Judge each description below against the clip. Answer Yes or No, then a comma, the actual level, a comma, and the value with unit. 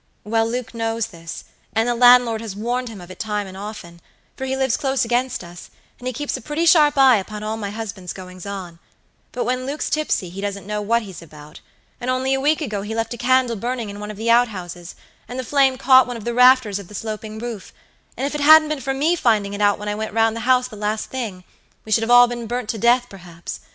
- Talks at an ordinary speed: No, fast, 255 wpm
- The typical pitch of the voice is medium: No, high, 225 Hz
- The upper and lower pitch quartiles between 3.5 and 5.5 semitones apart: Yes, average, 3.8 semitones